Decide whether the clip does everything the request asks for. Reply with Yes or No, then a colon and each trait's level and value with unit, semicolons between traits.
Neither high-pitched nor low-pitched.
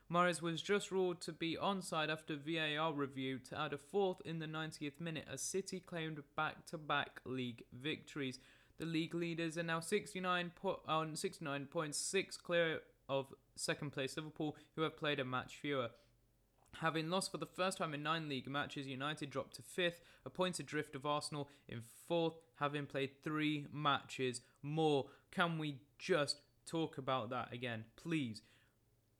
Yes: medium, 150 Hz